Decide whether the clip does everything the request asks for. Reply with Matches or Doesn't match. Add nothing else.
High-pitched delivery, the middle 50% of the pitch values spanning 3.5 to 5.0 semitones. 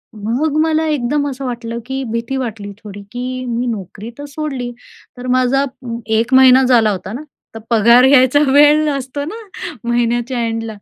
Doesn't match